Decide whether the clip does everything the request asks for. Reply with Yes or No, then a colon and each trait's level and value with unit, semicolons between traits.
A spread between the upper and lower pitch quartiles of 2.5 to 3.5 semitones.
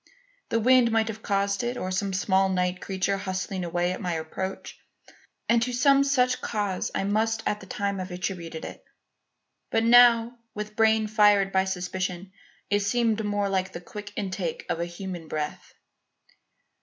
Yes: average, 3.1 semitones